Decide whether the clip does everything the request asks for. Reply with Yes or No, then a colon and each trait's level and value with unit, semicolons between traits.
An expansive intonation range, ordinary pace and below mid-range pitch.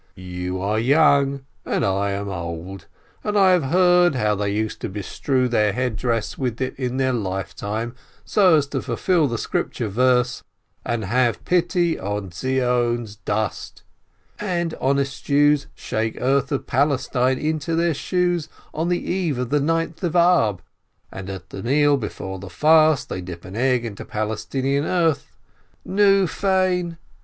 Yes: wide, 7.0 semitones; average, 160 wpm; low, 130 Hz